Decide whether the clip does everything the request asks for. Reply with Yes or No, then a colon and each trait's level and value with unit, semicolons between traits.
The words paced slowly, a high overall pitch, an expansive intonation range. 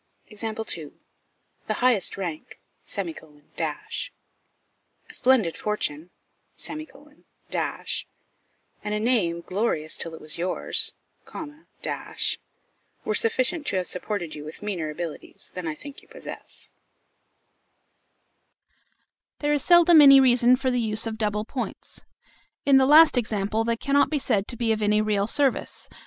Yes: slow, 120 wpm; high, 220 Hz; wide, 6.3 semitones